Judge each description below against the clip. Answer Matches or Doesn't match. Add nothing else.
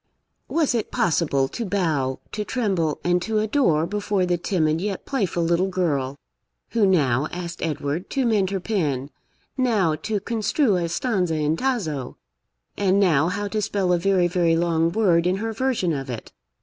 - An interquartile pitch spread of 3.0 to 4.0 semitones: Doesn't match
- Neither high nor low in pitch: Matches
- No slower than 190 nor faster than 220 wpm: Doesn't match